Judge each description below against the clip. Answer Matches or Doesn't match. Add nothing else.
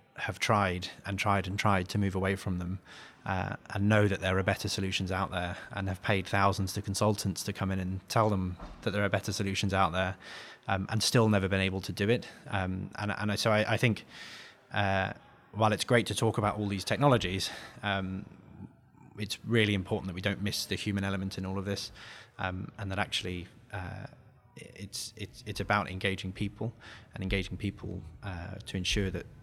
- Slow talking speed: Doesn't match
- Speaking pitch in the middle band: Doesn't match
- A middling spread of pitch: Doesn't match